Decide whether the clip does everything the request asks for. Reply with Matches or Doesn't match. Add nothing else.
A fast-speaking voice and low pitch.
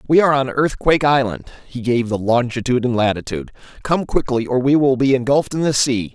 Matches